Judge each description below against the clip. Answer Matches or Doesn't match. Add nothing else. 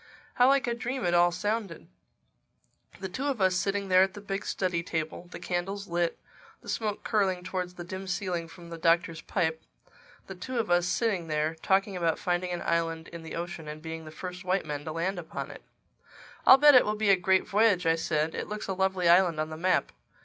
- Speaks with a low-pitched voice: Doesn't match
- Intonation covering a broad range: Doesn't match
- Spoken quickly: Matches